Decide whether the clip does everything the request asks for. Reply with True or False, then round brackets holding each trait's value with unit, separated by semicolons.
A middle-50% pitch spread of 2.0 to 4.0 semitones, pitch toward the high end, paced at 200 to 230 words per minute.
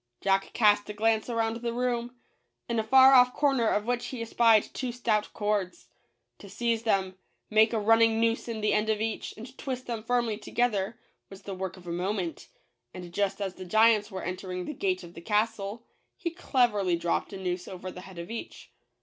True (3.4 semitones; 215 Hz; 205 wpm)